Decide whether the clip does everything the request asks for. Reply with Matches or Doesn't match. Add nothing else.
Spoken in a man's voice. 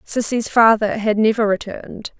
Doesn't match